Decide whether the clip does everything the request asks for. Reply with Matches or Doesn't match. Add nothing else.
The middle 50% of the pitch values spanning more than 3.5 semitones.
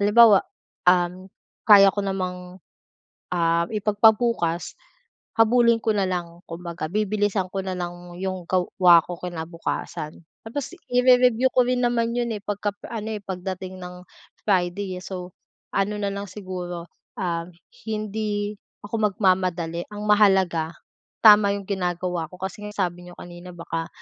Doesn't match